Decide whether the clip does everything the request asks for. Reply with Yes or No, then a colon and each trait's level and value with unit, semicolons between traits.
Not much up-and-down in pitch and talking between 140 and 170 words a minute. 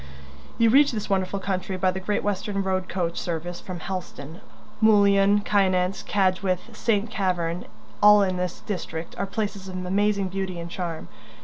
Yes: narrow, 1.9 semitones; average, 155 wpm